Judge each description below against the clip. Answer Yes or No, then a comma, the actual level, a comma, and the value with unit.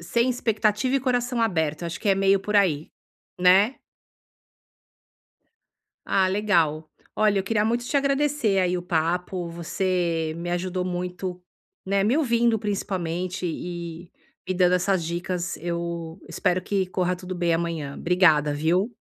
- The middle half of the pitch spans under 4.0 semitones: Yes, average, 3.3 semitones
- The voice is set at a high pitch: No, medium, 180 Hz